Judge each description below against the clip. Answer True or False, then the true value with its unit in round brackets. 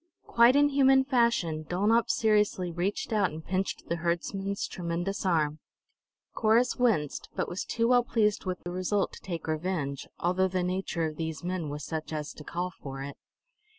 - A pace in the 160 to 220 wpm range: True (175 wpm)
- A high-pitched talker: False (180 Hz)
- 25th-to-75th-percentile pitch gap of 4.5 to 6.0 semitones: True (4.8 semitones)